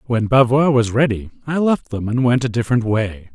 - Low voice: Yes, low, 120 Hz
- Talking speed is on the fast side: Yes, fast, 215 wpm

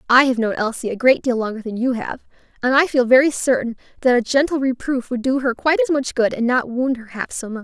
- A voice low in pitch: No, very high, 250 Hz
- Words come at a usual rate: No, fast, 265 wpm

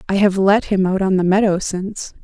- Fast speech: Yes, fast, 240 wpm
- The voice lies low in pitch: No, high, 195 Hz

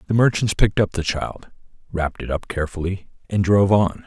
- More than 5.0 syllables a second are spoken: Yes, 6.0 syllables/s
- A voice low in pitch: Yes, very low, 95 Hz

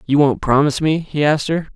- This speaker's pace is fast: Yes, fast, 240 wpm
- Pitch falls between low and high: Yes, medium, 145 Hz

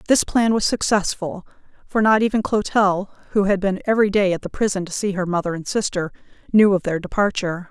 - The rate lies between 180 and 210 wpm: Yes, average, 200 wpm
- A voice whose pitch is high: Yes, high, 195 Hz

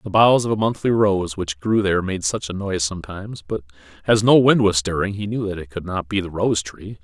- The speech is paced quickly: Yes, fast, 255 wpm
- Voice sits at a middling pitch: No, very low, 95 Hz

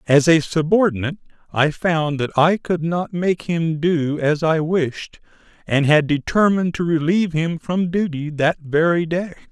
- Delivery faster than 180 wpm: No, average, 165 wpm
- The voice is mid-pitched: Yes, medium, 160 Hz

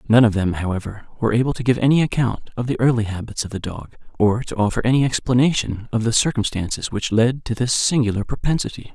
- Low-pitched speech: Yes, low, 115 Hz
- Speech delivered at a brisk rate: Yes, fast, 210 wpm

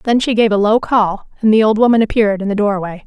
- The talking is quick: Yes, fast, 275 wpm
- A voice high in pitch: Yes, high, 215 Hz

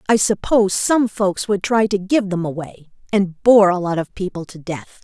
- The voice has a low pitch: No, high, 195 Hz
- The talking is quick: Yes, fast, 215 wpm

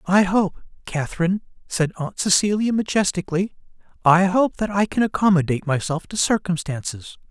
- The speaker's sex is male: Yes, male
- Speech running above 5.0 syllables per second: Yes, 5.4 syllables/s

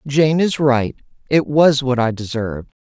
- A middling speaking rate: Yes, average, 170 wpm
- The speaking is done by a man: Yes, male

